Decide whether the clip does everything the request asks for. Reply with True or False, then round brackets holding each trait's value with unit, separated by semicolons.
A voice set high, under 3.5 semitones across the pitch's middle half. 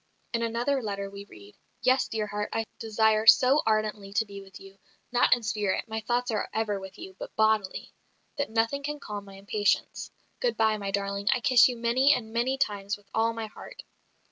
True (220 Hz; 2.9 semitones)